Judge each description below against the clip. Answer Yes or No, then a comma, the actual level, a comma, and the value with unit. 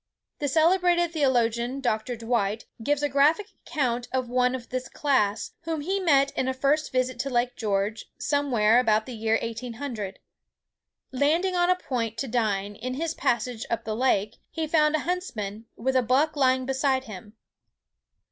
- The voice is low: No, very high, 255 Hz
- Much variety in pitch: No, average, 4.3 semitones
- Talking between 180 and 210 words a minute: No, average, 165 wpm